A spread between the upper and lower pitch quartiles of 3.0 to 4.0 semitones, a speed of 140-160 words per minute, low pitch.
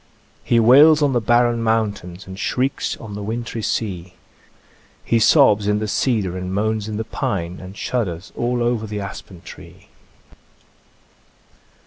Yes: average, 3.5 semitones; average, 145 wpm; low, 110 Hz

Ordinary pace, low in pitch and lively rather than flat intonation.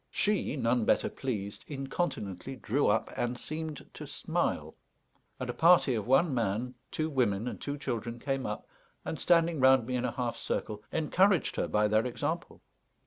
No: average, 170 wpm; low, 130 Hz; average, 4.7 semitones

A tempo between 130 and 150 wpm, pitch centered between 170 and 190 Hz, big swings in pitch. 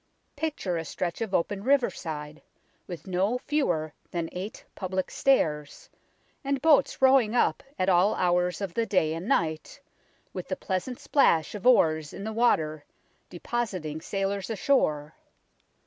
Yes: average, 140 wpm; medium, 185 Hz; wide, 6.5 semitones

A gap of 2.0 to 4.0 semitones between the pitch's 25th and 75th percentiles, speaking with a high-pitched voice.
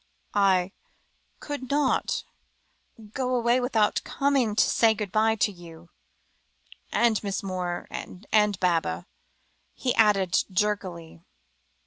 No: average, 4.4 semitones; high, 210 Hz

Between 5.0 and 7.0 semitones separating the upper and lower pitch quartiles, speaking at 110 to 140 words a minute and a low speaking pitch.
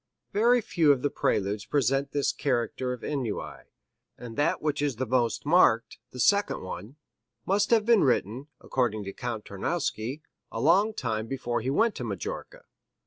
No: wide, 5.4 semitones; average, 165 wpm; low, 130 Hz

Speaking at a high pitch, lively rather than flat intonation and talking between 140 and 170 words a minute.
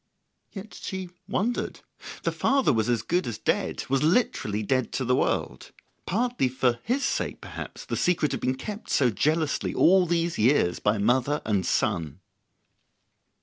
No: low, 135 Hz; wide, 7.6 semitones; average, 155 wpm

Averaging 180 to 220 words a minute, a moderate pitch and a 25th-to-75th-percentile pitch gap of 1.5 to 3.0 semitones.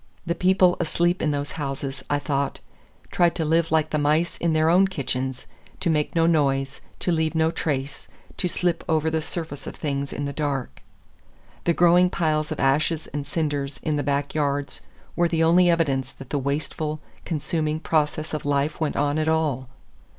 Yes: average, 185 wpm; medium, 155 Hz; narrow, 2.6 semitones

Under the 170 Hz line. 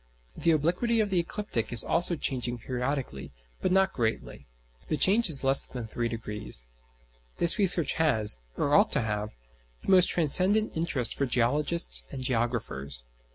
Yes: medium, 140 Hz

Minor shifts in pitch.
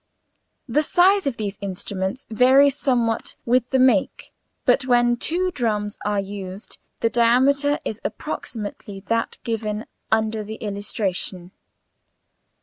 No: average, 4.0 semitones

